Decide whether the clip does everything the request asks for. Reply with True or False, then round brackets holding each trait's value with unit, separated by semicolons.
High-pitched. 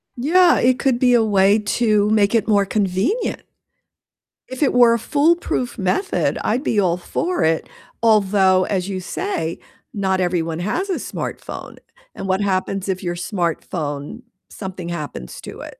True (200 Hz)